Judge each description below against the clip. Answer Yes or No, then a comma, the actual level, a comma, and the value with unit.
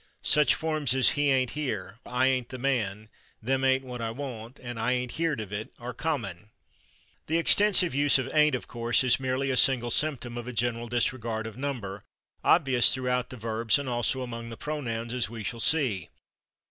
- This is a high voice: No, low, 125 Hz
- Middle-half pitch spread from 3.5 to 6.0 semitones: No, average, 2.8 semitones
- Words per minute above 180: Yes, average, 195 wpm